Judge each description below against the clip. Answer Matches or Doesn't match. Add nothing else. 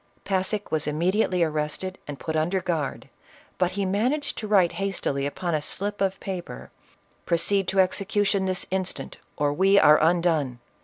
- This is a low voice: Doesn't match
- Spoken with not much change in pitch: Doesn't match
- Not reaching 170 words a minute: Matches